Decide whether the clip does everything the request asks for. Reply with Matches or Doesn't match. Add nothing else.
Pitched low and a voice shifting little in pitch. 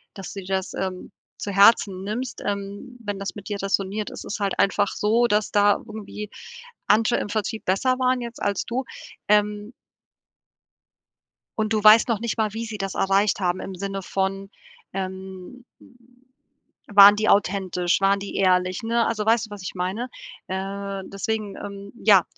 Doesn't match